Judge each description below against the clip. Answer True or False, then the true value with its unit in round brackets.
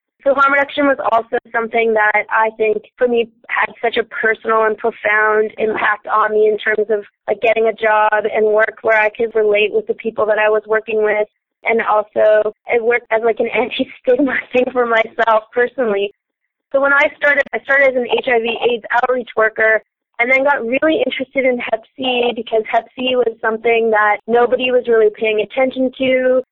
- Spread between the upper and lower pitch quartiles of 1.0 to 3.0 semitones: True (2.7 semitones)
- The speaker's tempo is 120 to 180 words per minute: False (190 wpm)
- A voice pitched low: False (230 Hz)